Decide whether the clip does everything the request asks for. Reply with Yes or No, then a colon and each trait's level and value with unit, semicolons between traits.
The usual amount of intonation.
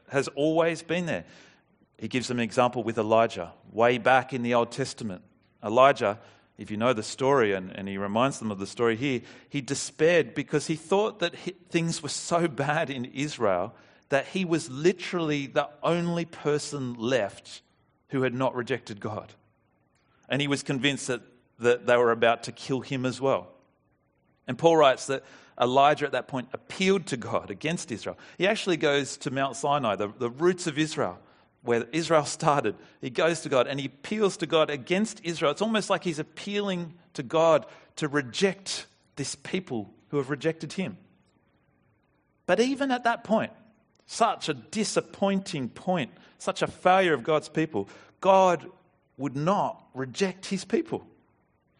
No: wide, 5.8 semitones